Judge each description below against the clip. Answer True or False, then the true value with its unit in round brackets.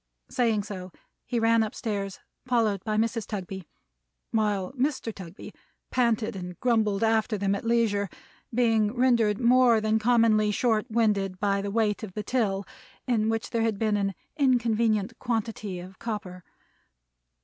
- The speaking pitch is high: True (215 Hz)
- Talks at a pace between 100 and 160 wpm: True (150 wpm)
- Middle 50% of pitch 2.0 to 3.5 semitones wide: True (2.5 semitones)